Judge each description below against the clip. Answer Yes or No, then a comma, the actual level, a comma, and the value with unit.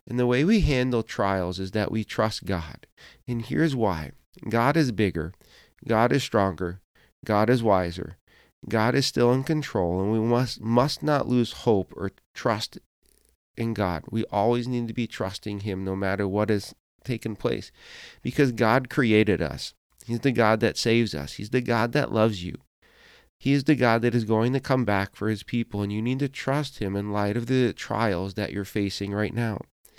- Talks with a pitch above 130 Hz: No, low, 110 Hz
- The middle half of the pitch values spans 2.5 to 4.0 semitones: Yes, average, 3.5 semitones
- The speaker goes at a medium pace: Yes, average, 195 wpm